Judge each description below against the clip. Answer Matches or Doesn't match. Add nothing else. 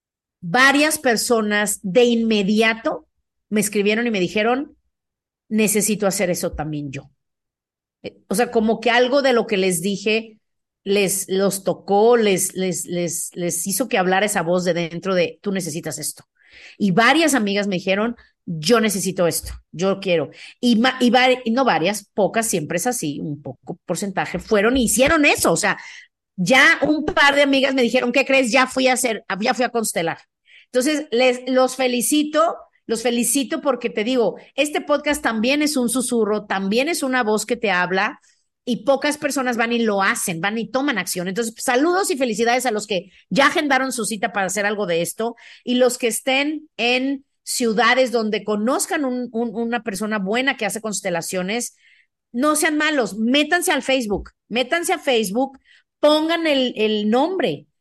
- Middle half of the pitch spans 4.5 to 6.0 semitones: Matches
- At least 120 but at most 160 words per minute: Doesn't match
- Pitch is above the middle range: Matches